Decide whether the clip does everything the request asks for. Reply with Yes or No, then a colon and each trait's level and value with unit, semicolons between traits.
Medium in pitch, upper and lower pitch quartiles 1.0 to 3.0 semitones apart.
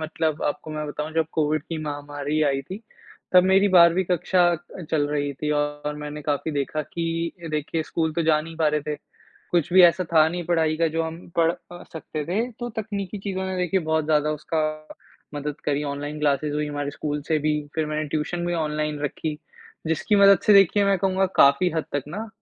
Yes: medium, 155 Hz; average, 2.7 semitones